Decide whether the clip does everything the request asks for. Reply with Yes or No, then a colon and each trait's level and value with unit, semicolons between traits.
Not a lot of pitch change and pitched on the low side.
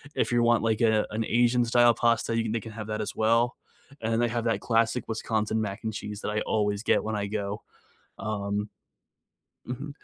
Yes: narrow, 1.6 semitones; low, 110 Hz